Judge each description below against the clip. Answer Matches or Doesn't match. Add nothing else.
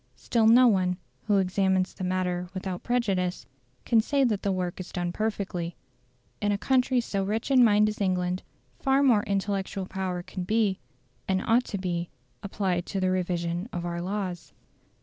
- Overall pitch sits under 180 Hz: Doesn't match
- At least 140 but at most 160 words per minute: Doesn't match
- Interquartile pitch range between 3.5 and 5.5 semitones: Doesn't match